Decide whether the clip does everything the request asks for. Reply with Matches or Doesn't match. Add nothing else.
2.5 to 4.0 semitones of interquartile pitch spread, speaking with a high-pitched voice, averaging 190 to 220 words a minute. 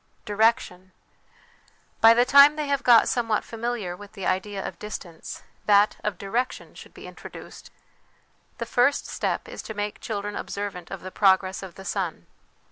Doesn't match